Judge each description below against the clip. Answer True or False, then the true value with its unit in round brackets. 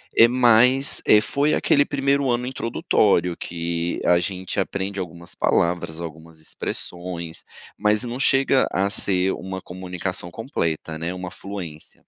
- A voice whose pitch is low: True (95 Hz)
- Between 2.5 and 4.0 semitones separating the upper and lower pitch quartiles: False (5.5 semitones)